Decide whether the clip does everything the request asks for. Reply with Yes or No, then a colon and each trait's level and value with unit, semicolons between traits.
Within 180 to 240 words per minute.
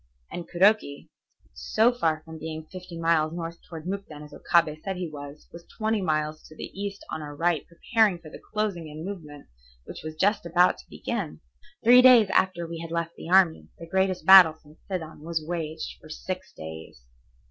Yes: average, 190 wpm